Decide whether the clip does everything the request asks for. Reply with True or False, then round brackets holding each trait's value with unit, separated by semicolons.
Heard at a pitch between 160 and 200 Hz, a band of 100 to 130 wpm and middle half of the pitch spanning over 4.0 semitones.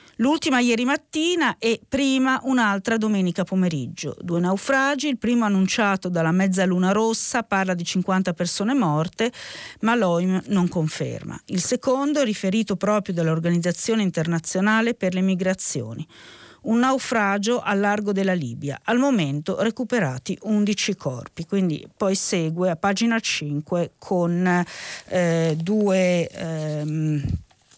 True (190 Hz; 120 wpm; 4.8 semitones)